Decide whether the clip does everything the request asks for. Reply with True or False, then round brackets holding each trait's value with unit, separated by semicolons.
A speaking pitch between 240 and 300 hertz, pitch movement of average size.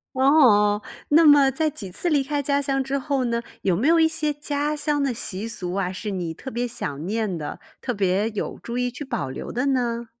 False (245 Hz; 5.7 semitones)